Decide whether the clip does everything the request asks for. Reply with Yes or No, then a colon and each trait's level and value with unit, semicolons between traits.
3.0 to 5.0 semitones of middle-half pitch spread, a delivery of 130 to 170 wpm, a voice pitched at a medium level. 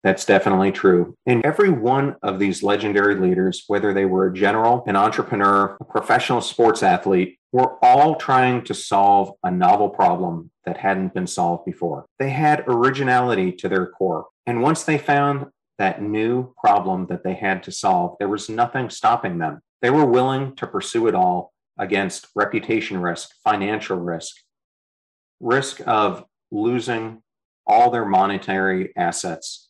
No: average, 4.7 semitones; average, 155 wpm; low, 100 Hz